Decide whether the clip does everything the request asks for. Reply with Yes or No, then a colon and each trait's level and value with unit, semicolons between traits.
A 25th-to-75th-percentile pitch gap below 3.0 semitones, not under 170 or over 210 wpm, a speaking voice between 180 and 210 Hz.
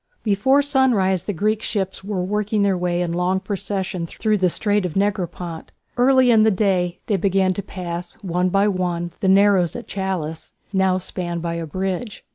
Yes: narrow, 2.6 semitones; average, 180 wpm; high, 190 Hz